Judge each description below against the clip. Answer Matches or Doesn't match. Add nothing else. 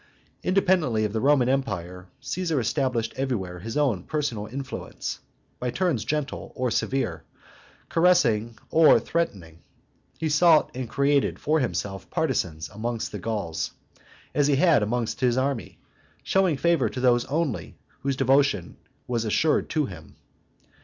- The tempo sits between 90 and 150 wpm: Matches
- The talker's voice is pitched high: Doesn't match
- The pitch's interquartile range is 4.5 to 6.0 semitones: Matches